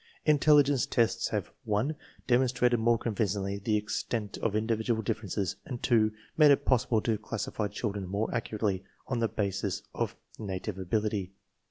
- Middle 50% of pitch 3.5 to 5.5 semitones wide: No, average, 2.9 semitones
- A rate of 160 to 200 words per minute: No, average, 150 wpm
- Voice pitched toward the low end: Yes, low, 110 Hz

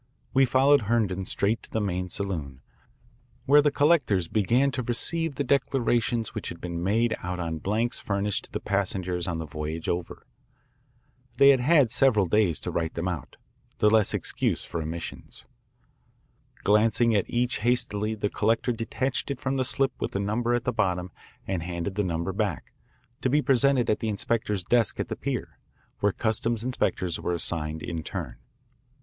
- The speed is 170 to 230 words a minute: Yes, average, 175 wpm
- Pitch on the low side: Yes, low, 105 Hz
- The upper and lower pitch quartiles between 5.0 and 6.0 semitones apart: Yes, average, 5.3 semitones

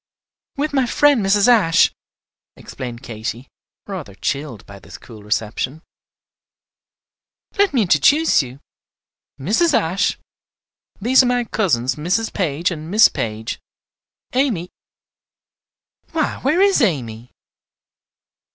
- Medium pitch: Yes, medium, 175 Hz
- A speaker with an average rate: No, slow, 105 wpm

